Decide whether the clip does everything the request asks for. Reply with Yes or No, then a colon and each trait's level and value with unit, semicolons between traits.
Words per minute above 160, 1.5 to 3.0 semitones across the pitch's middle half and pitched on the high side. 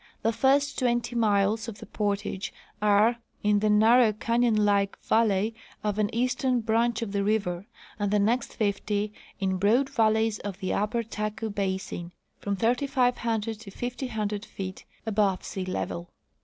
No: average, 150 wpm; narrow, 2.5 semitones; high, 215 Hz